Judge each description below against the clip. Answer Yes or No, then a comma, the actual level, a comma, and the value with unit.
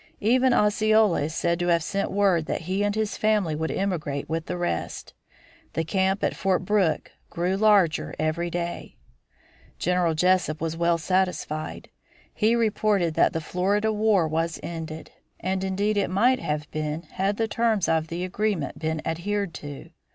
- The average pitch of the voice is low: No, medium, 180 Hz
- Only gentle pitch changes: No, average, 4.0 semitones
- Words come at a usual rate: Yes, average, 165 wpm